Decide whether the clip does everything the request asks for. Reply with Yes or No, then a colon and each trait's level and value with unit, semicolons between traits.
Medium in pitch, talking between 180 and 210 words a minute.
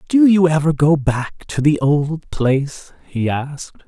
No: medium, 150 Hz; average, 170 wpm